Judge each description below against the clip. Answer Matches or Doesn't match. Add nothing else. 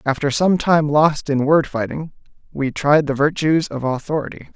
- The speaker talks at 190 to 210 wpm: Doesn't match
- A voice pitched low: Doesn't match